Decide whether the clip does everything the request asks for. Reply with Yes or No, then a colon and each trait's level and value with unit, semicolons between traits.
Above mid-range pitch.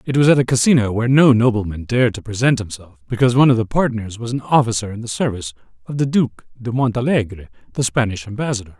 No: low, 115 Hz